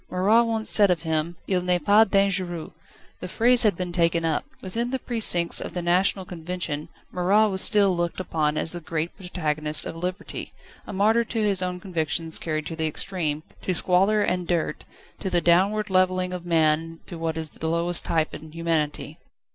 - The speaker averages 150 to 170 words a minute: No, average, 185 wpm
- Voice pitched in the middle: Yes, medium, 180 Hz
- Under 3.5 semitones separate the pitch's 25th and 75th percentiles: Yes, average, 3.0 semitones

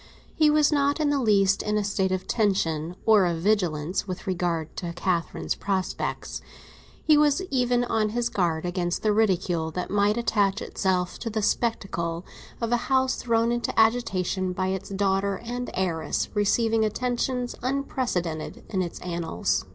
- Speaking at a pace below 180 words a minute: Yes, average, 160 wpm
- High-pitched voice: Yes, high, 200 Hz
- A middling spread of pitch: Yes, average, 4.9 semitones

